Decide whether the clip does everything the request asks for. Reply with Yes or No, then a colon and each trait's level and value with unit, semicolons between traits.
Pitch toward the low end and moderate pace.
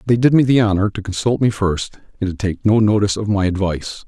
No: low, 105 Hz; fast, 250 wpm